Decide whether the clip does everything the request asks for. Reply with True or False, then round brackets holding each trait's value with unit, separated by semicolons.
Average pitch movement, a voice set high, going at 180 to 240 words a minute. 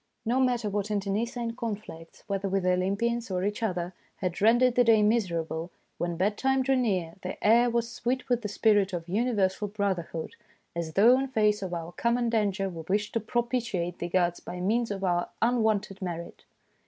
True (4.4 semitones; 205 Hz; 195 wpm)